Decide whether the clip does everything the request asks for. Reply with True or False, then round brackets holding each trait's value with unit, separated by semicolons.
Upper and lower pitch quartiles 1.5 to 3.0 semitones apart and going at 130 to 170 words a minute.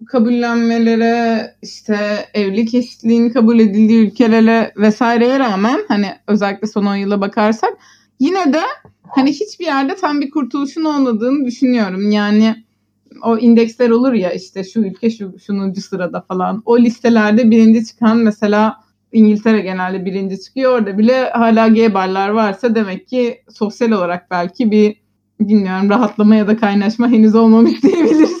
True (2.5 semitones; 140 wpm)